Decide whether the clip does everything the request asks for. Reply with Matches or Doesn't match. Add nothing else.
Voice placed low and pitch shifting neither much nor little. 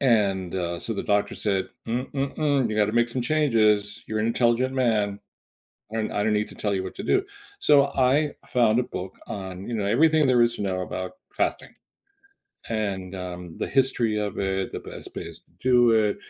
Matches